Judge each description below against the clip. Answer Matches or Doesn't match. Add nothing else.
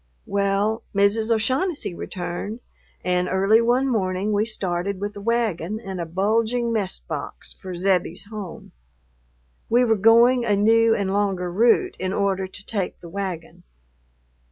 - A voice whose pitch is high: Matches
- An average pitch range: Matches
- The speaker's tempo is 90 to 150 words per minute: Matches